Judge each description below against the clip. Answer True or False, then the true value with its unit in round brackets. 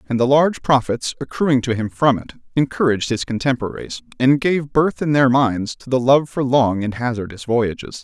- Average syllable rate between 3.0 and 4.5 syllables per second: False (5.3 syllables/s)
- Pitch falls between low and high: False (130 Hz)